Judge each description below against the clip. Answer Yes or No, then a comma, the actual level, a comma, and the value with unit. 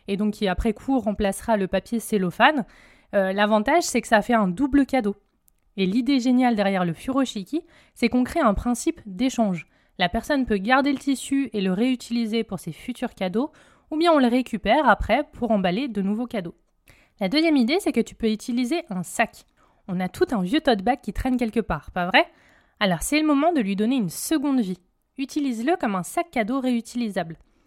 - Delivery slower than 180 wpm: No, average, 200 wpm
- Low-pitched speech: No, high, 235 Hz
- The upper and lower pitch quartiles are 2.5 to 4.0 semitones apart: No, average, 5.1 semitones